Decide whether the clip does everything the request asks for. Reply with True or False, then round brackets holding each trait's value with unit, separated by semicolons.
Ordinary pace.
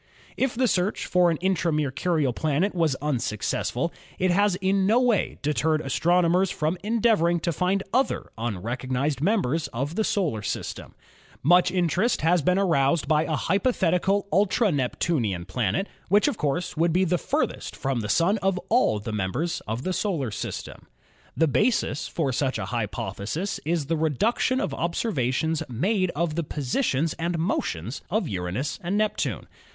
True (160 wpm)